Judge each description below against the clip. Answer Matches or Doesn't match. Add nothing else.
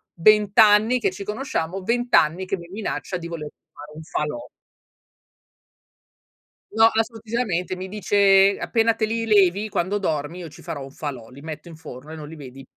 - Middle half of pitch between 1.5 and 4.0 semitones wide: Doesn't match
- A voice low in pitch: Doesn't match